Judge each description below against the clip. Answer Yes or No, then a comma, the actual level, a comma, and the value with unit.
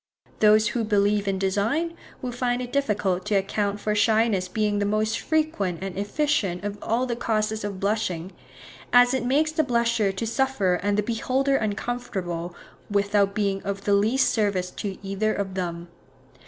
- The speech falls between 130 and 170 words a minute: Yes, average, 165 wpm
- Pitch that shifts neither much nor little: Yes, average, 3.1 semitones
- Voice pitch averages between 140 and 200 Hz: No, high, 210 Hz